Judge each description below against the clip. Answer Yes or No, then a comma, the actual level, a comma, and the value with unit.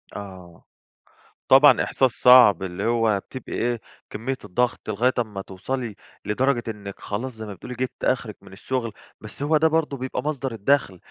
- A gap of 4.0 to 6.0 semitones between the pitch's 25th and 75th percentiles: Yes, average, 4.3 semitones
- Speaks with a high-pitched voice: No, low, 115 Hz